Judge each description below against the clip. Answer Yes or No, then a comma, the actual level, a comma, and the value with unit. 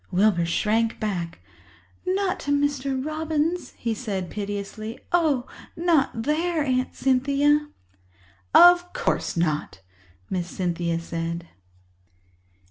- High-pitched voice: Yes, very high, 255 Hz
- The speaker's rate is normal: No, slow, 100 wpm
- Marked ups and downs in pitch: Yes, wide, 8.2 semitones